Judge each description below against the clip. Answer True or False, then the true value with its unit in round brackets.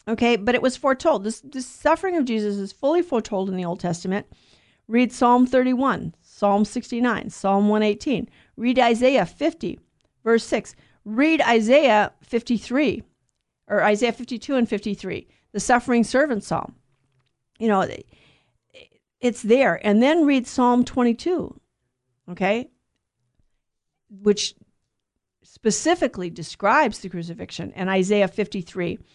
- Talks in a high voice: True (220 Hz)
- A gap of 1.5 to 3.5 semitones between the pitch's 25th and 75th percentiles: False (4.9 semitones)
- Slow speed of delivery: True (125 wpm)